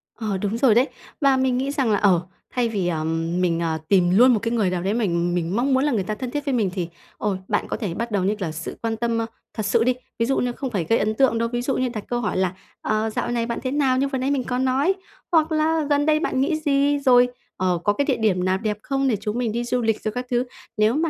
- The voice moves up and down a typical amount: Yes, average, 4.5 semitones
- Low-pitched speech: No, high, 230 Hz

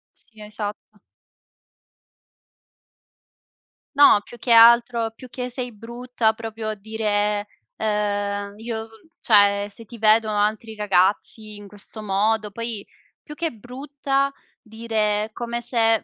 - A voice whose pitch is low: No, high, 220 Hz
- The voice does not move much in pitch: Yes, narrow, 2.1 semitones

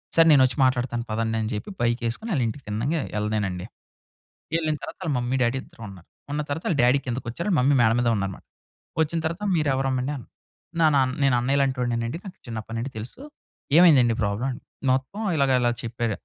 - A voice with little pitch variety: No, average, 3.8 semitones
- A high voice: No, low, 125 Hz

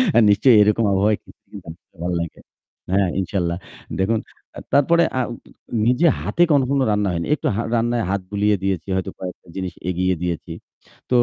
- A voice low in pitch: Yes, low, 100 Hz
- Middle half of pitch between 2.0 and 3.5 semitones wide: No, average, 4.1 semitones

